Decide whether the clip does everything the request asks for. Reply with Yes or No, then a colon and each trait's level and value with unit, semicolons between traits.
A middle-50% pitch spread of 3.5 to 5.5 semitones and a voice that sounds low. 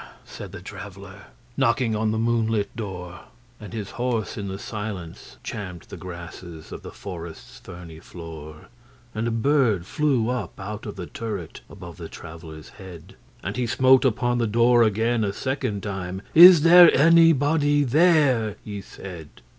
Yes: average, 5.1 semitones; low, 110 Hz